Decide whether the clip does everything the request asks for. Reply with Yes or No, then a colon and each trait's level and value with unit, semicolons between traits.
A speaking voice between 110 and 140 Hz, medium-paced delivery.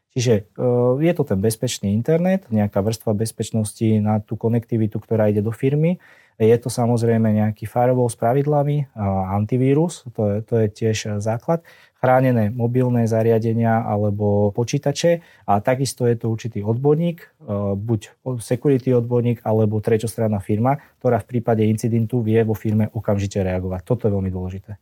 Yes: low, 115 Hz; average, 145 wpm